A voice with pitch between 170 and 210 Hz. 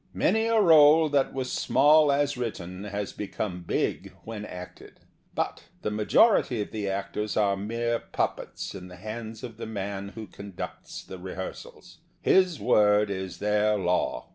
No: low, 105 Hz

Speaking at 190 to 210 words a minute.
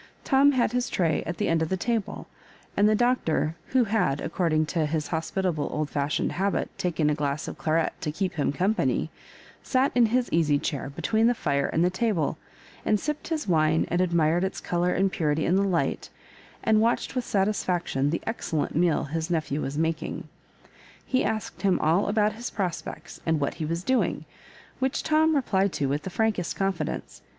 Yes: average, 195 wpm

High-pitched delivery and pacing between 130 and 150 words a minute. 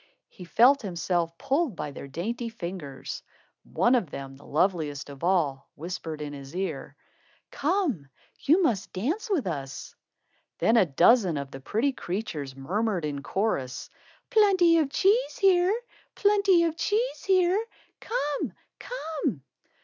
Yes: high, 205 Hz; slow, 135 wpm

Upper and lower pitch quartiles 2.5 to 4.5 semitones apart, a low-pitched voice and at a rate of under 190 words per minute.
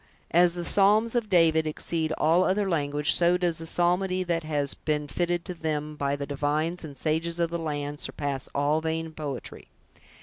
No: average, 2.8 semitones; medium, 160 Hz; average, 180 wpm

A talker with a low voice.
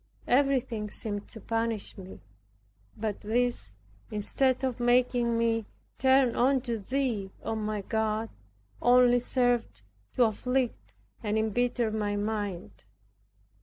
No: high, 230 Hz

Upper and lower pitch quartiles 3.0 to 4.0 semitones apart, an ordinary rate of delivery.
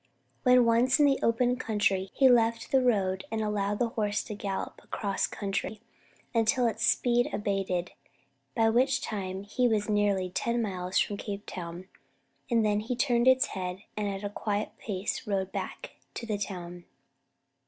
Yes: average, 3.3 semitones; average, 165 wpm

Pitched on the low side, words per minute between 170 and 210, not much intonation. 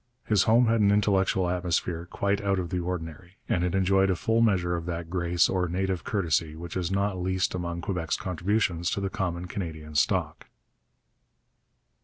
Yes: very low, 90 Hz; average, 175 wpm; narrow, 2.2 semitones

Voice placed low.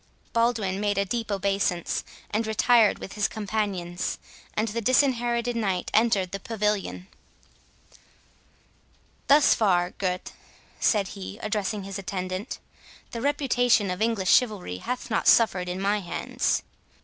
No: high, 210 Hz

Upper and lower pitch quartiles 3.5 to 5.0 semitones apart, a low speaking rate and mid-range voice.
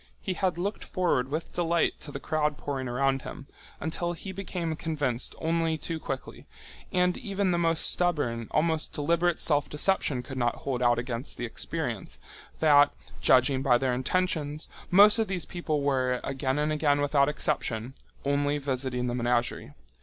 No: average, 4.4 semitones; average, 155 wpm; medium, 145 Hz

